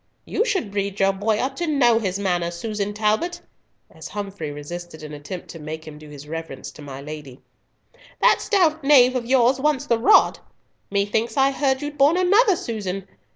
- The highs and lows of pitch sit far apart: Yes, wide, 8.0 semitones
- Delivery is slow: No, average, 185 wpm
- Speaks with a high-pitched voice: Yes, high, 210 Hz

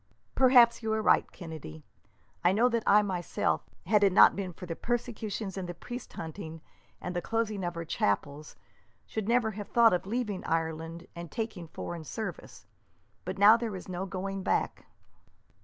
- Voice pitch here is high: Yes, high, 195 Hz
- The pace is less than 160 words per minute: No, average, 175 wpm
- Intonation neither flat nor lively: Yes, average, 4.6 semitones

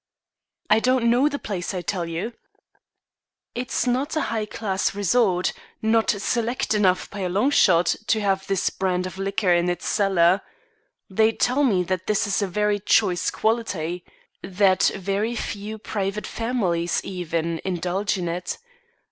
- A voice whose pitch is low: No, high, 195 Hz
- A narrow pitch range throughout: No, average, 3.5 semitones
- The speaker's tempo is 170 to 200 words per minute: No, average, 155 wpm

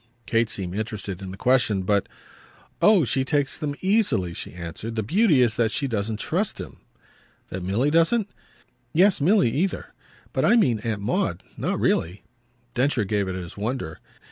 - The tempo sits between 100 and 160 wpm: No, average, 170 wpm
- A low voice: Yes, low, 115 Hz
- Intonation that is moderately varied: No, wide, 6.6 semitones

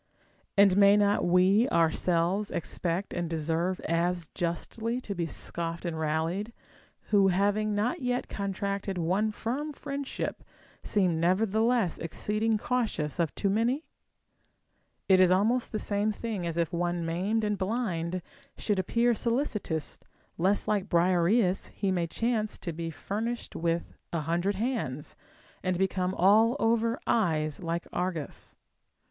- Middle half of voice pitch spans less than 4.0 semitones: No, average, 4.3 semitones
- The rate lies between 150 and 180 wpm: No, slow, 135 wpm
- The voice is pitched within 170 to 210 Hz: Yes, high, 190 Hz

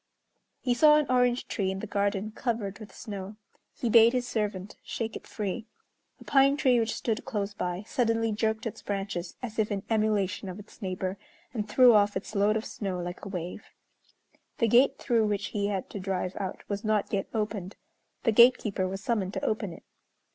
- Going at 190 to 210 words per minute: Yes, average, 195 wpm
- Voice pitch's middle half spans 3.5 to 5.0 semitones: No, average, 2.7 semitones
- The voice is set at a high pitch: Yes, high, 210 Hz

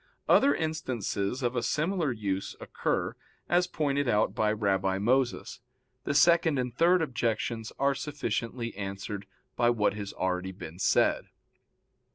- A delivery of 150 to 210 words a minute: No, slow, 135 wpm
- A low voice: Yes, low, 120 Hz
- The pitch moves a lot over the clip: Yes, wide, 6.2 semitones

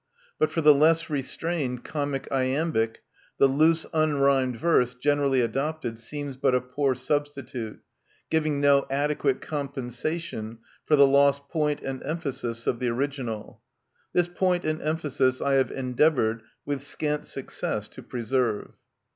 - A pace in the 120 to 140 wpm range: Yes, slow, 135 wpm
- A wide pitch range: No, average, 3.1 semitones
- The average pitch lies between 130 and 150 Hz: Yes, medium, 140 Hz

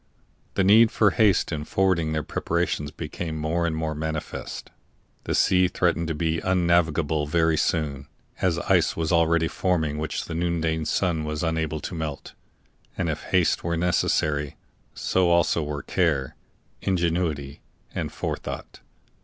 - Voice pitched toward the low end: Yes, very low, 80 Hz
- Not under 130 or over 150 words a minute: Yes, average, 145 wpm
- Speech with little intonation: Yes, narrow, 2.0 semitones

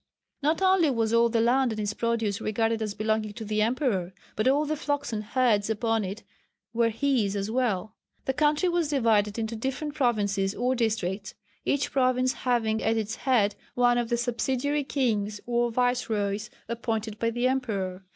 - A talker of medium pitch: No, high, 230 Hz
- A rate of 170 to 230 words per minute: Yes, average, 175 wpm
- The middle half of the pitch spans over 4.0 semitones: No, average, 3.2 semitones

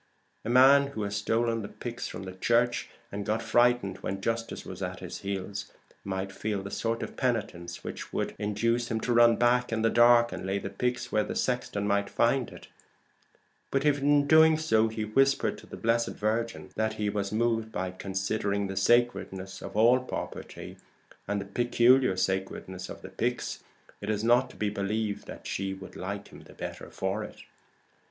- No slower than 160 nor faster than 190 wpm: Yes, average, 185 wpm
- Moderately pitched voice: No, low, 110 Hz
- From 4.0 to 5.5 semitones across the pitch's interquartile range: No, average, 3.2 semitones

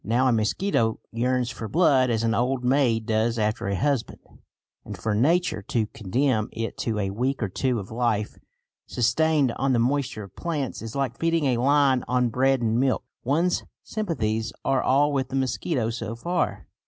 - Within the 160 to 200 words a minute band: Yes, average, 180 wpm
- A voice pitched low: Yes, low, 125 Hz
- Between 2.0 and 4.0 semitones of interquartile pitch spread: Yes, average, 3.4 semitones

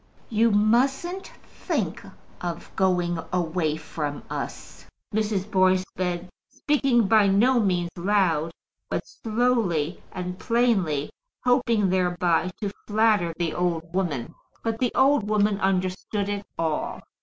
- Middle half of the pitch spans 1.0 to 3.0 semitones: No, average, 4.2 semitones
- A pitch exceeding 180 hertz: Yes, high, 190 Hz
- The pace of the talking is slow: Yes, slow, 120 wpm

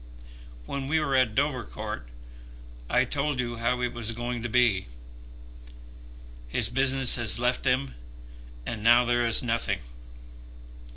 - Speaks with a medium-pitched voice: No, low, 120 Hz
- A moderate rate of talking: No, slow, 130 wpm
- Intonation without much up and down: Yes, narrow, 2.2 semitones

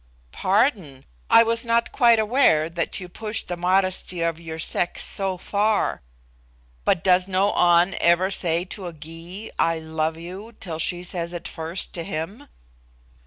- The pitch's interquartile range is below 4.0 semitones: Yes, average, 3.4 semitones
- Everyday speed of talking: Yes, average, 160 wpm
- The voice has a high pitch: No, medium, 180 Hz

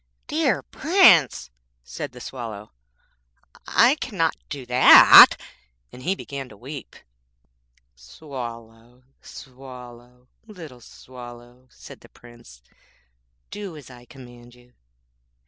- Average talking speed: No, slow, 95 wpm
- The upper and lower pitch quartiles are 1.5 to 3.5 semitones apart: Yes, average, 3.1 semitones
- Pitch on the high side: No, low, 125 Hz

